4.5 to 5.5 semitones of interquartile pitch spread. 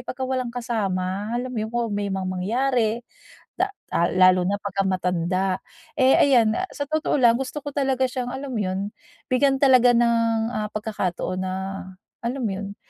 Yes: average, 5.0 semitones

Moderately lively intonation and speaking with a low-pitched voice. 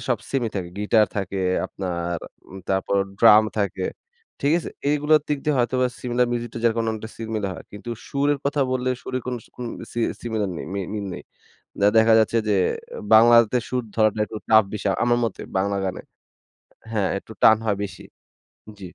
Yes: average, 3.4 semitones; low, 110 Hz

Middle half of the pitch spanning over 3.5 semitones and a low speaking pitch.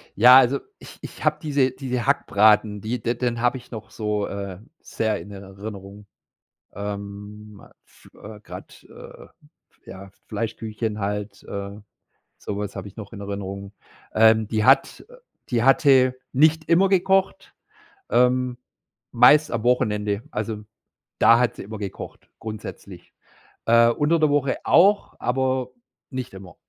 Yes: average, 3.9 semitones; low, 110 Hz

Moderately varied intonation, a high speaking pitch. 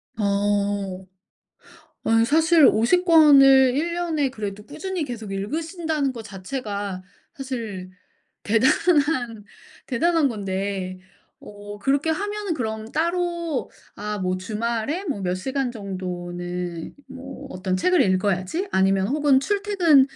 No: wide, 7.7 semitones; high, 235 Hz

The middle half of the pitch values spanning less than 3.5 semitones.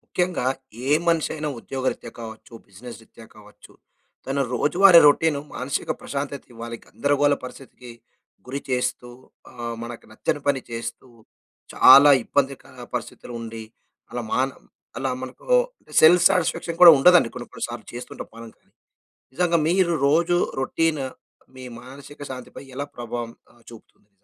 No: average, 3.8 semitones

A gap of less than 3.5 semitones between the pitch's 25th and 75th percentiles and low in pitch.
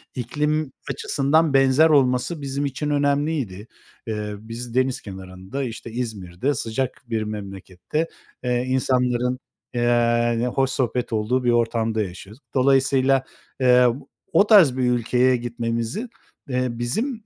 Yes: average, 2.9 semitones; low, 125 Hz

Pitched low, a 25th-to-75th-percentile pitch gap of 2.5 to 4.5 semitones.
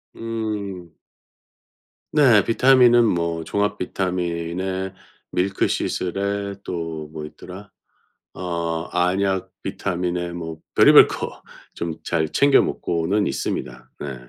Yes: very low, 90 Hz; average, 3.2 semitones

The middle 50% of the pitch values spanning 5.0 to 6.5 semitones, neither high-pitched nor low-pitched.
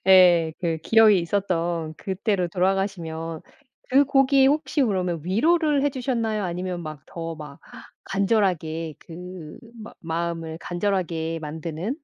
No: average, 4.5 semitones; medium, 180 Hz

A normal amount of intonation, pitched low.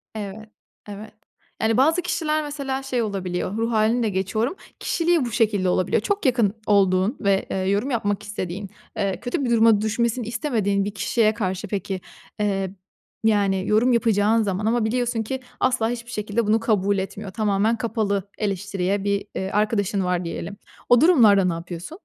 No: average, 3.0 semitones; high, 210 Hz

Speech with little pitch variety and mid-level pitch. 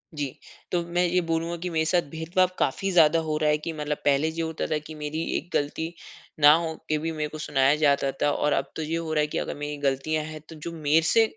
Yes: narrow, 1.8 semitones; medium, 155 Hz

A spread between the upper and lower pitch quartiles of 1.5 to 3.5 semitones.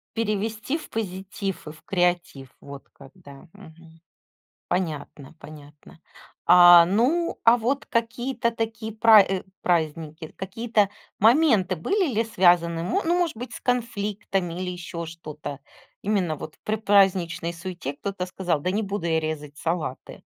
No: average, 5.2 semitones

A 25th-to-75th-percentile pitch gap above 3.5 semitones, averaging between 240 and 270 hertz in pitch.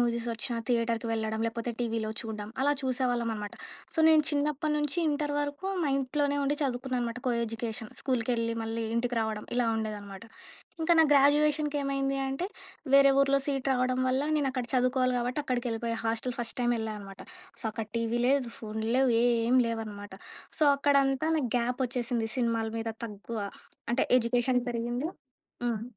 No: average, 3.1 semitones; high, 245 Hz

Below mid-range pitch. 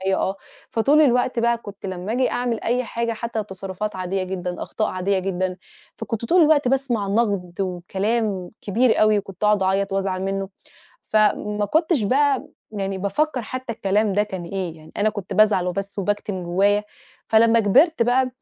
No: high, 205 Hz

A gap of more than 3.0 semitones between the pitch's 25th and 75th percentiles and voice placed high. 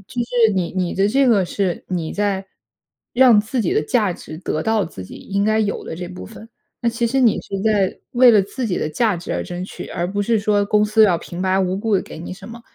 Yes: average, 3.5 semitones; high, 205 Hz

